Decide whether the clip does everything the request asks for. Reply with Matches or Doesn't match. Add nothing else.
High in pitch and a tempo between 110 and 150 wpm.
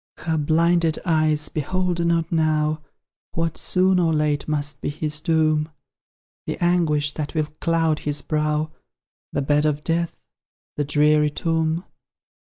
Doesn't match